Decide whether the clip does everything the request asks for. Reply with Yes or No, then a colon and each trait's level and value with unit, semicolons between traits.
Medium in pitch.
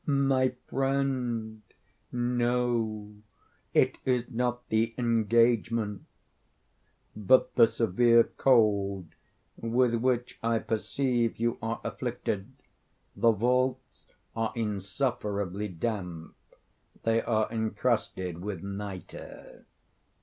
No: low, 115 Hz